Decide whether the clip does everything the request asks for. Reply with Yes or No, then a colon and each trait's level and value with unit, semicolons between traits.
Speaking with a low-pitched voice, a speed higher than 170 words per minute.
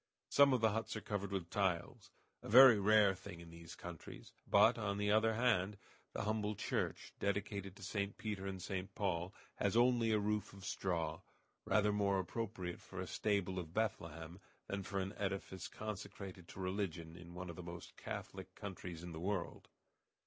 Yes: low, 100 Hz; average, 180 wpm